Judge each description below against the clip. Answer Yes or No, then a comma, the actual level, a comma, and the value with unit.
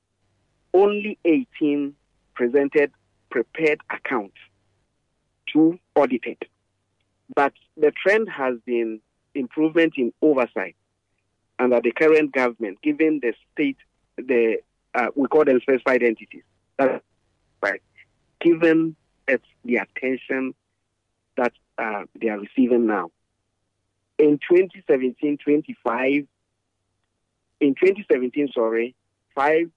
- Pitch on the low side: Yes, low, 130 Hz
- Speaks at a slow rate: Yes, slow, 95 wpm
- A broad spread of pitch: Yes, wide, 6.3 semitones